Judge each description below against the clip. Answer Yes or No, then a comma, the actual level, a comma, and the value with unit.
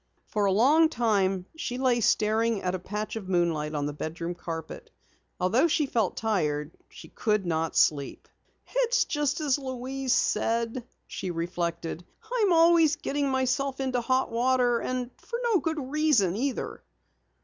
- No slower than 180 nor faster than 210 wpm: No, average, 150 wpm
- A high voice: Yes, high, 235 Hz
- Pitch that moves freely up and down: Yes, wide, 6.9 semitones